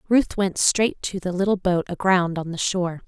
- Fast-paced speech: Yes, fast, 215 wpm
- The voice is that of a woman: Yes, female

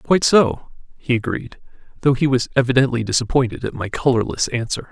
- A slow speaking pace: No, average, 160 wpm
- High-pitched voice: No, low, 125 Hz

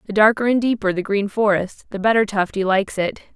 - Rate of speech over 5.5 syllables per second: Yes, 5.9 syllables/s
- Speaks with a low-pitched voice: No, high, 205 Hz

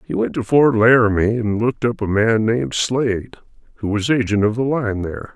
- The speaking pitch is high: No, low, 110 Hz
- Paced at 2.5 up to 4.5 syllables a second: No, 5.5 syllables/s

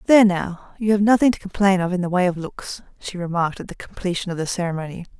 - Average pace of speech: No, fast, 245 wpm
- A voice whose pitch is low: No, medium, 185 Hz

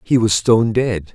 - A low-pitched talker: Yes, low, 110 Hz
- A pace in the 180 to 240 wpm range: Yes, fast, 210 wpm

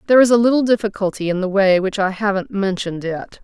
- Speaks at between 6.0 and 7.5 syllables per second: Yes, 6.5 syllables/s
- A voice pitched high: Yes, high, 200 Hz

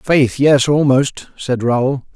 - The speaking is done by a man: Yes, male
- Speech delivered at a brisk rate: No, average, 140 wpm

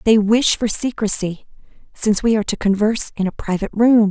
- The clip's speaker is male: No, female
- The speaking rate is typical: Yes, average, 190 wpm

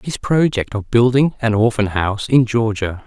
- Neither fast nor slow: Yes, average, 175 wpm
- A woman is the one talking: No, male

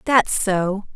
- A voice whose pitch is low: No, high, 205 Hz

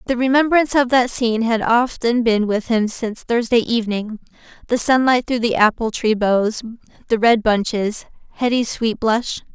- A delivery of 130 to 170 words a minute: Yes, average, 165 wpm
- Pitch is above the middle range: Yes, high, 230 Hz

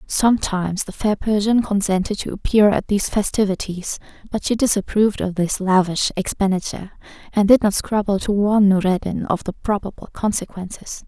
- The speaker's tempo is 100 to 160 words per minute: Yes, average, 150 wpm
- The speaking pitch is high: Yes, high, 200 Hz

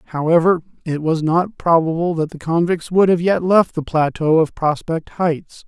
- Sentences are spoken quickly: No, average, 180 wpm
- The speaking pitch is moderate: Yes, medium, 165 Hz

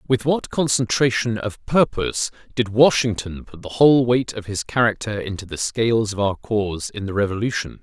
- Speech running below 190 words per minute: Yes, average, 175 wpm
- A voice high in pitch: No, low, 110 Hz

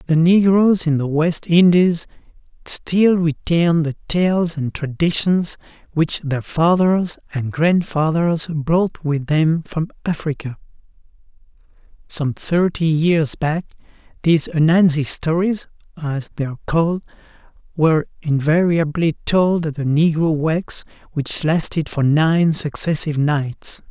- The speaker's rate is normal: No, slow, 115 wpm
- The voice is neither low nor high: Yes, medium, 160 Hz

